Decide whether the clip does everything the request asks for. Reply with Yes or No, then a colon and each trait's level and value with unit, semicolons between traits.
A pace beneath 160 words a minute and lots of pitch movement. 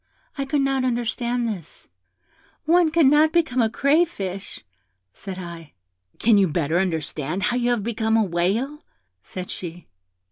Yes: average, 140 wpm; wide, 6.9 semitones